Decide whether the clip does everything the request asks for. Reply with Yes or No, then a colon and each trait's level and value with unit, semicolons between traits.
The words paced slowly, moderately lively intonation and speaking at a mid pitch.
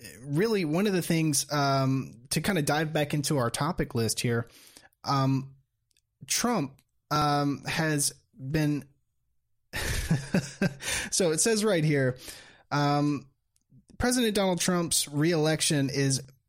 Yes: slow, 115 wpm; average, 3.1 semitones; medium, 145 Hz